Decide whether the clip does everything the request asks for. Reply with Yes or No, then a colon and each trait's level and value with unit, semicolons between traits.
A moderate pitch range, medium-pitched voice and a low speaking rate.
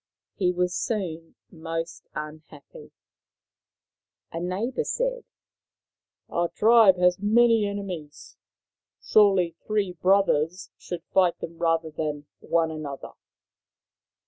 Yes: average, 3.7 semitones; medium, 180 Hz; slow, 100 wpm